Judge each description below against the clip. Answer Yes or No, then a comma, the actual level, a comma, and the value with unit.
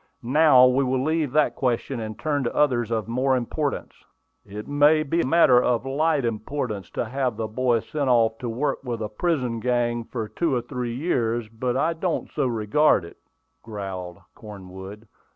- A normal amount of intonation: Yes, average, 4.0 semitones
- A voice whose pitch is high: No, low, 125 Hz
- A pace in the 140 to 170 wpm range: No, average, 180 wpm